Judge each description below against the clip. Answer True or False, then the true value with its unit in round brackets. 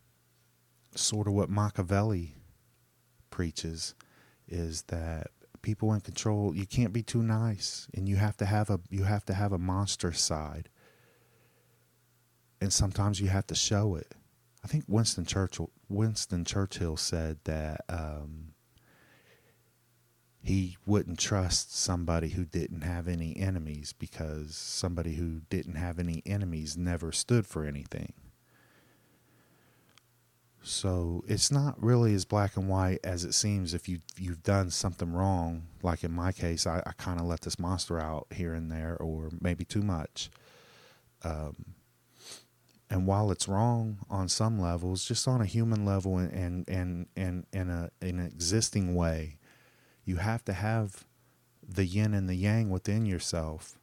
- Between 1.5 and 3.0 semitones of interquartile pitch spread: False (3.7 semitones)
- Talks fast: False (145 wpm)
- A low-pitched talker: True (95 Hz)